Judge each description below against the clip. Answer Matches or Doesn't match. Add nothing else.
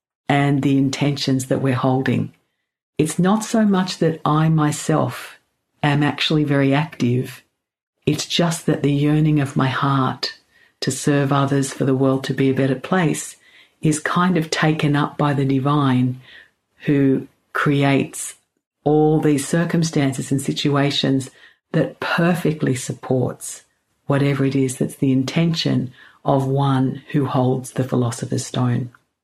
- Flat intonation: Matches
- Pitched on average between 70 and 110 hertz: Doesn't match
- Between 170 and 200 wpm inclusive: Doesn't match